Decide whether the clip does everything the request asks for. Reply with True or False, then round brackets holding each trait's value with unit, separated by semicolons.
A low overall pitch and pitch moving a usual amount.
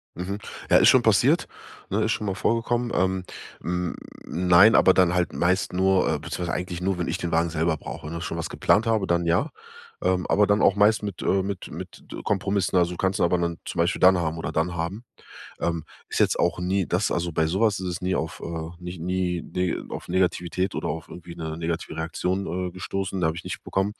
False (90 Hz; 2.1 semitones)